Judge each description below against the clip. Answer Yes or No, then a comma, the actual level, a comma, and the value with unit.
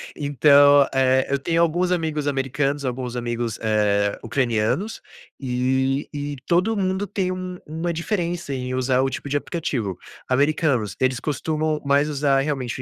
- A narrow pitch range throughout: No, average, 3.8 semitones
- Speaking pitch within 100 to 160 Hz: Yes, medium, 140 Hz